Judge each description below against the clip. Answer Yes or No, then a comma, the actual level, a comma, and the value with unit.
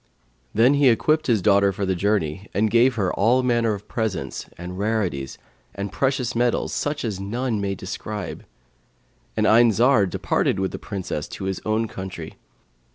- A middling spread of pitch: Yes, average, 3.6 semitones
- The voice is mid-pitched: No, low, 105 Hz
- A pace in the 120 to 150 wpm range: No, average, 165 wpm